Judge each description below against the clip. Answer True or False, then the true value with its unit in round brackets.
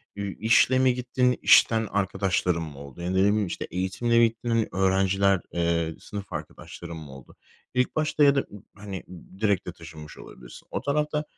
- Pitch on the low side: True (100 Hz)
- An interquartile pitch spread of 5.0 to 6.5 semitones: True (5.4 semitones)